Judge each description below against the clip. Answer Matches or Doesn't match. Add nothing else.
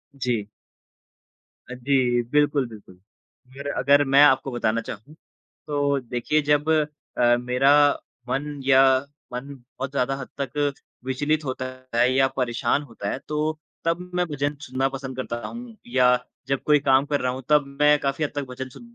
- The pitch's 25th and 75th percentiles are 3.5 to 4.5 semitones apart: Doesn't match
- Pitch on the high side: Doesn't match